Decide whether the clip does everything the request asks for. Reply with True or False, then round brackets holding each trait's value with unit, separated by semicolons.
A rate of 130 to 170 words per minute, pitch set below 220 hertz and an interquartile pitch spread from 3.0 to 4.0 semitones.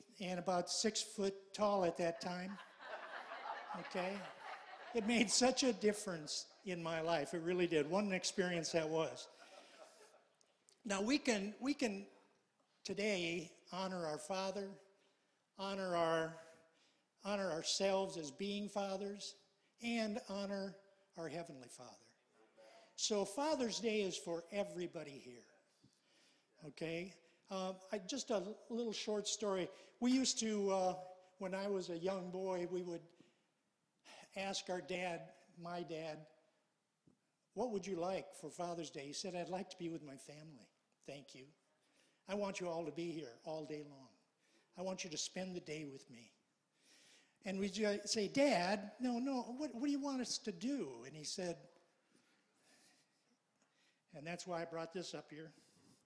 True (150 wpm; 185 Hz; 3.4 semitones)